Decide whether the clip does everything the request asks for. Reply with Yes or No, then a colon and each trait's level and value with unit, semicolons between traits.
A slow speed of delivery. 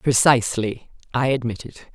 Yes: slow, 95 wpm